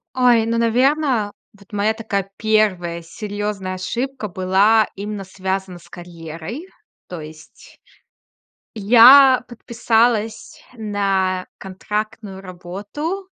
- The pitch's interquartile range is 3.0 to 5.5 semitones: Yes, average, 3.7 semitones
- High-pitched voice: Yes, high, 205 Hz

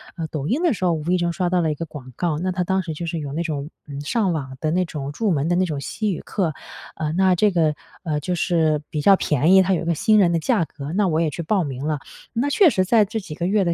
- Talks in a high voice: No, medium, 170 Hz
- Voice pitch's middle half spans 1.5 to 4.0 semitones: Yes, average, 3.7 semitones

